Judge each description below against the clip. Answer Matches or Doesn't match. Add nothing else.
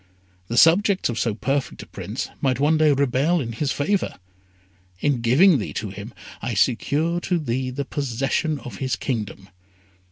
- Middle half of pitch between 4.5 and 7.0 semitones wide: Matches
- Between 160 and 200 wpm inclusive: Matches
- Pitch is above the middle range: Doesn't match